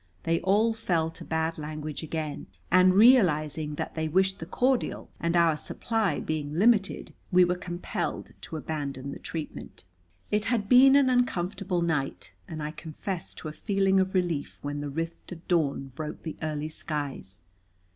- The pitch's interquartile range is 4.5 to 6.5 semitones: No, average, 4.0 semitones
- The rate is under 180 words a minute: Yes, average, 165 wpm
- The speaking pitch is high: No, medium, 165 Hz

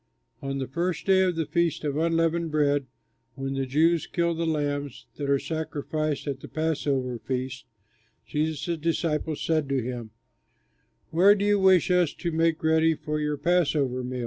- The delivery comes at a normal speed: Yes, average, 170 wpm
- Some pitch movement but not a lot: Yes, average, 3.2 semitones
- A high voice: No, medium, 155 Hz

